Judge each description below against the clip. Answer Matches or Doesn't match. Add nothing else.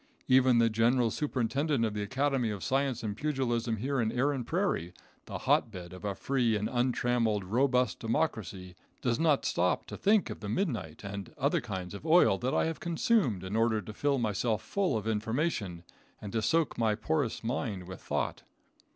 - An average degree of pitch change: Matches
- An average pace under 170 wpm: Doesn't match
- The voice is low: Matches